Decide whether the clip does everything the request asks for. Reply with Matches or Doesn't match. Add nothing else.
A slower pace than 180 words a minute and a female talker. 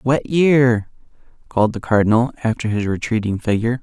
Doesn't match